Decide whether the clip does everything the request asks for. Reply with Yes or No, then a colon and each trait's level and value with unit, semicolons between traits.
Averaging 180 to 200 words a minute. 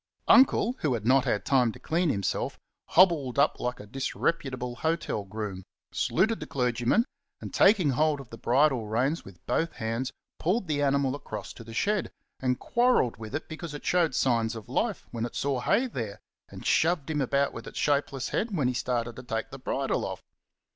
Yes: average, 195 wpm